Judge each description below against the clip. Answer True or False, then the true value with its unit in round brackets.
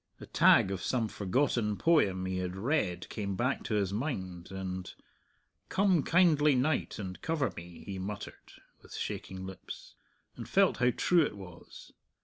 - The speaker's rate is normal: True (155 wpm)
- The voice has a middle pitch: False (105 Hz)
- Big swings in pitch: True (7.2 semitones)